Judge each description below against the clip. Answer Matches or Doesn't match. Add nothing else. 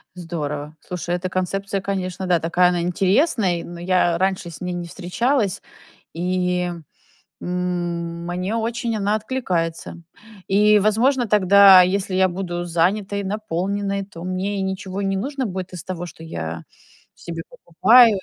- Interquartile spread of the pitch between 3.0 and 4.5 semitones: Doesn't match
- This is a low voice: Doesn't match